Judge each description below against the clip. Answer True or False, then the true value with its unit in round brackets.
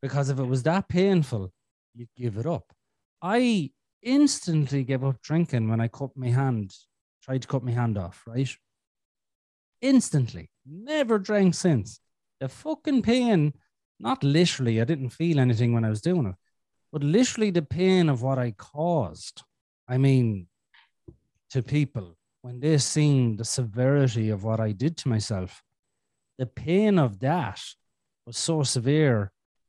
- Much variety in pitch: True (6.3 semitones)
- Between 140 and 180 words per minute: True (150 wpm)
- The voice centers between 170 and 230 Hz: False (135 Hz)